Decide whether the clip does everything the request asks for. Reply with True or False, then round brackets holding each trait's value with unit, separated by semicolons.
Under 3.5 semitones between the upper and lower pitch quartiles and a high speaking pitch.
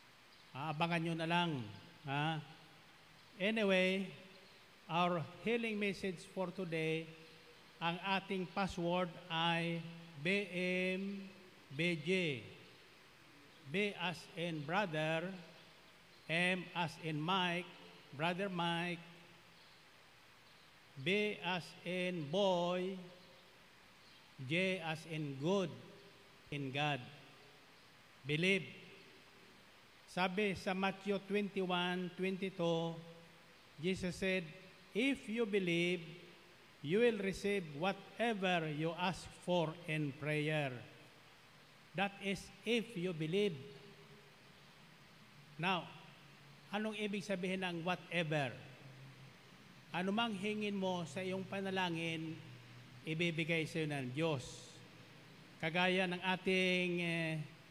False (3.0 semitones; 175 Hz)